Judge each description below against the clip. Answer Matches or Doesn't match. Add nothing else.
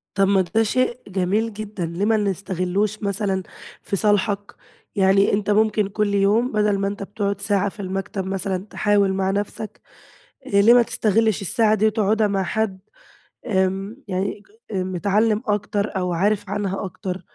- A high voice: Matches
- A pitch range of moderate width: Doesn't match